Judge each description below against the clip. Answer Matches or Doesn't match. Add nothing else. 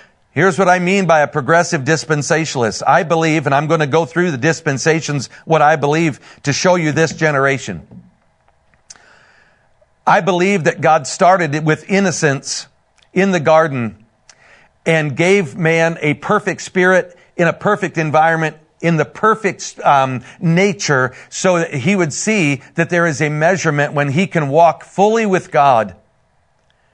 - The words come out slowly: Doesn't match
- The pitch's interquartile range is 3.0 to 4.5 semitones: Matches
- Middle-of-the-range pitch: Matches